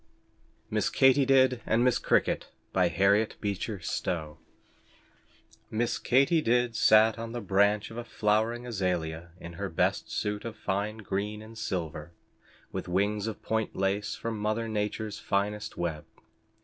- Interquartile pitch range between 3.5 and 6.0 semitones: No, average, 2.8 semitones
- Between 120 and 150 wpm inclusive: Yes, average, 140 wpm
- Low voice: Yes, low, 105 Hz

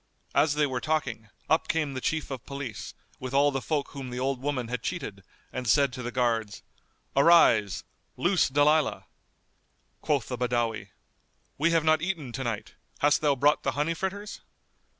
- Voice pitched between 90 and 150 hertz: Yes, medium, 140 Hz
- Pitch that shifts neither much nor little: Yes, average, 3.8 semitones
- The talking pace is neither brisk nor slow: Yes, average, 170 wpm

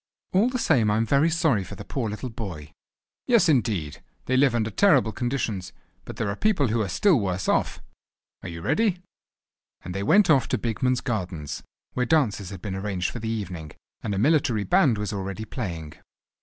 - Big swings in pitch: Yes, wide, 6.1 semitones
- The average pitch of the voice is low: Yes, low, 110 Hz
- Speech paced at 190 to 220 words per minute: Yes, average, 195 wpm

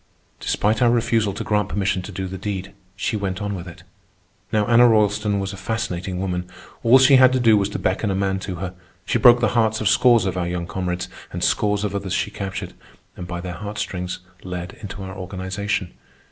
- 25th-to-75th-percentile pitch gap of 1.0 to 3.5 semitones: Yes, narrow, 2.6 semitones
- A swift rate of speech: Yes, fast, 215 wpm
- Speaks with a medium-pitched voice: No, low, 100 Hz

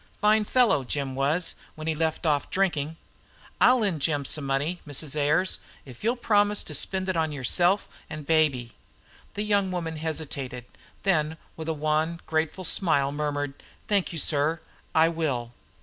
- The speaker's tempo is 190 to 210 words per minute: No, average, 160 wpm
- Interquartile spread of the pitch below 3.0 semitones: No, average, 4.0 semitones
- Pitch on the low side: No, medium, 160 Hz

